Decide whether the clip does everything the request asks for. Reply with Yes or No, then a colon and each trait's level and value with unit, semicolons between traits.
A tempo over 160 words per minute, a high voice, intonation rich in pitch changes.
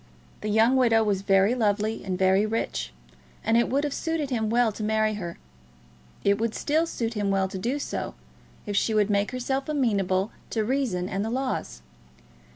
No: average, 185 wpm; high, 220 Hz; average, 3.7 semitones